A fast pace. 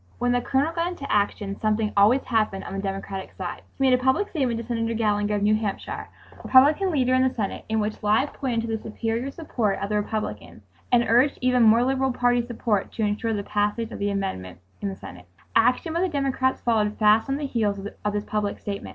Yes: fast, 220 wpm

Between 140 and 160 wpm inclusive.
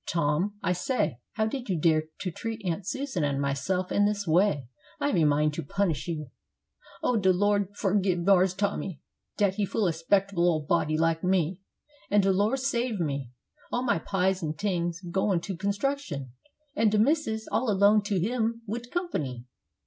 No: average, 180 wpm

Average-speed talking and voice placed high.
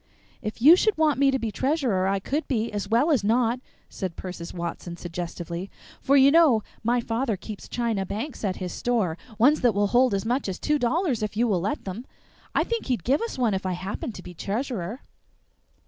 No: fast, 210 wpm; high, 225 Hz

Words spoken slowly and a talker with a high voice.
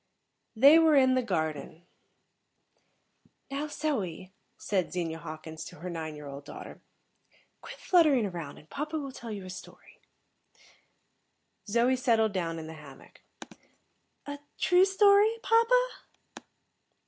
Yes: slow, 130 wpm; high, 220 Hz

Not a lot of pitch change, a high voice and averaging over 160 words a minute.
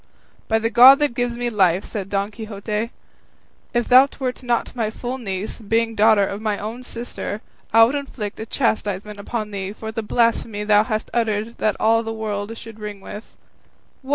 Yes: narrow, 2.2 semitones; high, 220 Hz; average, 185 wpm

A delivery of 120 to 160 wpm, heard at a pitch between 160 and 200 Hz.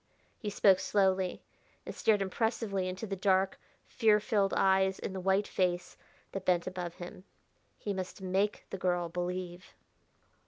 Yes: average, 150 wpm; high, 190 Hz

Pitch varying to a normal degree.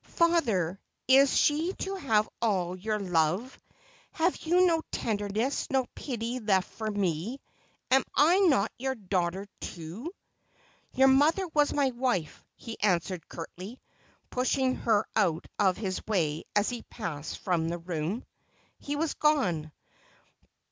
No: wide, 6.8 semitones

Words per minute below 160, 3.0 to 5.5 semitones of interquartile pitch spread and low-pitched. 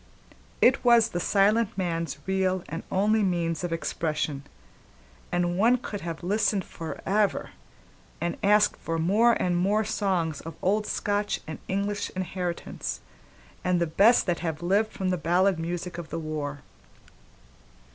No: average, 145 wpm; average, 3.5 semitones; medium, 185 Hz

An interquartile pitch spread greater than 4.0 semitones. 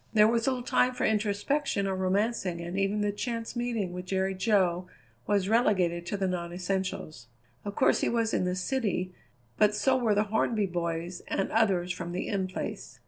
No: average, 3.5 semitones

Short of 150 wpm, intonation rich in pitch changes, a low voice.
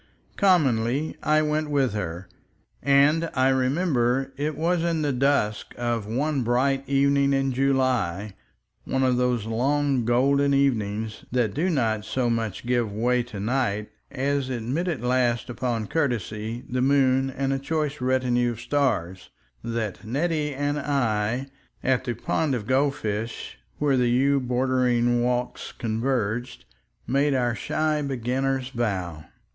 No: average, 140 wpm; average, 3.0 semitones; low, 130 Hz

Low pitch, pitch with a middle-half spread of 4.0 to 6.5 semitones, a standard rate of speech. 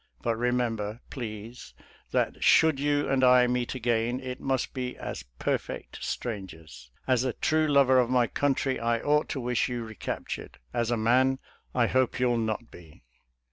No: low, 125 Hz; narrow, 2.4 semitones; average, 170 wpm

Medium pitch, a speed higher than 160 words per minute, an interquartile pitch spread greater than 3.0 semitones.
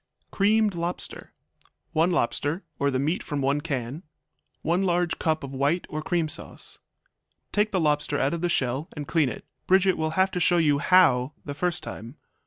Yes: medium, 160 Hz; average, 185 wpm; average, 3.9 semitones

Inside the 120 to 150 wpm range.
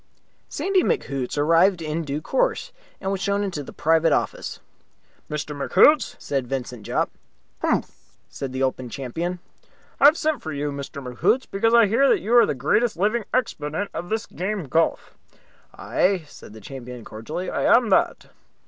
No: average, 170 wpm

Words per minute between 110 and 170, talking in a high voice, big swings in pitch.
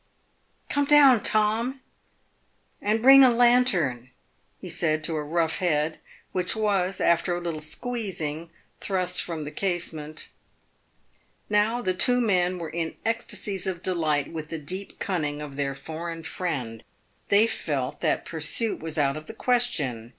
No: average, 155 wpm; medium, 175 Hz; wide, 5.8 semitones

